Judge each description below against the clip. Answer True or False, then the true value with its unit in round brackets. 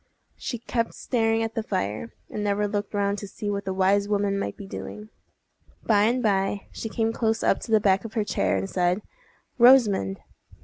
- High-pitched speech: True (205 Hz)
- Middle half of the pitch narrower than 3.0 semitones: True (2.4 semitones)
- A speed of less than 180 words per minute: False (195 wpm)